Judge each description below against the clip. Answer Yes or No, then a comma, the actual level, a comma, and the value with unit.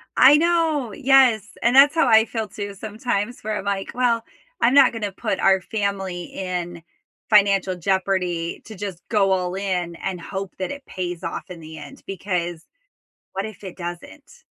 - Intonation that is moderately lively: Yes, average, 4.1 semitones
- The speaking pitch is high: Yes, high, 200 Hz